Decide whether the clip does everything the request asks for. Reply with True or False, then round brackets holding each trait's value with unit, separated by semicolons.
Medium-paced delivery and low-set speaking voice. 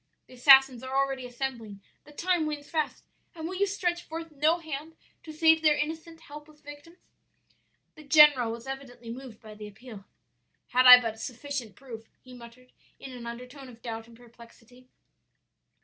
False (165 wpm; 265 Hz)